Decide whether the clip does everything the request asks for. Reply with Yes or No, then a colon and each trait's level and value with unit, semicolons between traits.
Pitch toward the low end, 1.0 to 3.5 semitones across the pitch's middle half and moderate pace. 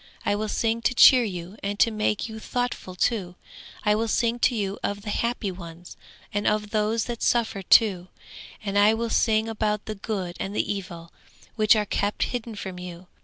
No: high, 210 Hz; narrow, 2.6 semitones; average, 190 wpm